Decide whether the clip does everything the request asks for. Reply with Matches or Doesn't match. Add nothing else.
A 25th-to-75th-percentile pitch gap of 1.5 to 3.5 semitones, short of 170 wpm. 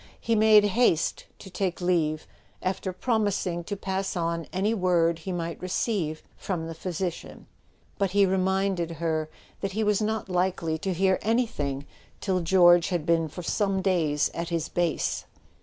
Matches